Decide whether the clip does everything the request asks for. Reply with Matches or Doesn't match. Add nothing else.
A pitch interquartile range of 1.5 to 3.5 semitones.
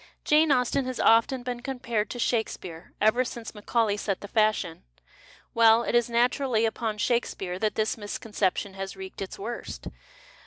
Matches